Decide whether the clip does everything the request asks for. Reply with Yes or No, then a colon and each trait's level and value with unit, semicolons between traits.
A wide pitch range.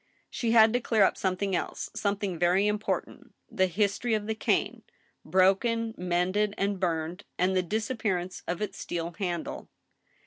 No: average, 3.0 semitones